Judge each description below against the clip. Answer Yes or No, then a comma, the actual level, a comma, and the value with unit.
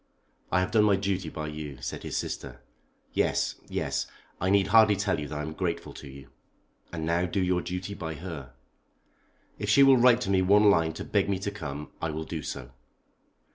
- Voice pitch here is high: No, very low, 90 Hz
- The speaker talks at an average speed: No, fast, 210 wpm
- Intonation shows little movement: No, average, 4.5 semitones